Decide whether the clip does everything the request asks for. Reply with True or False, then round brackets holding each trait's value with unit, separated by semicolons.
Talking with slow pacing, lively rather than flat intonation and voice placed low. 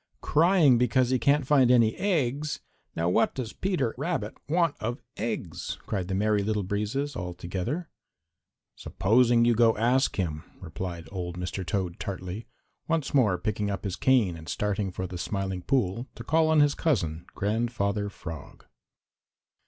False (155 wpm; 6.0 semitones; 110 Hz)